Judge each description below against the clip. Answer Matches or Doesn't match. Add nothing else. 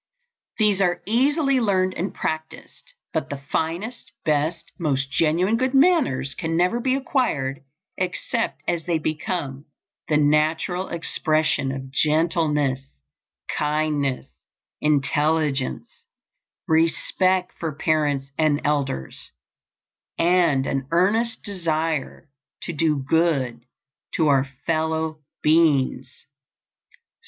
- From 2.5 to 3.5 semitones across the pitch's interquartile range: Doesn't match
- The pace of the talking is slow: Matches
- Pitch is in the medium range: Matches